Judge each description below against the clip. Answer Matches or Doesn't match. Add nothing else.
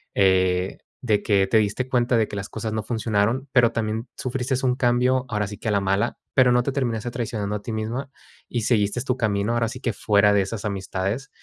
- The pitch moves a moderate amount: Matches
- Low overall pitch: Matches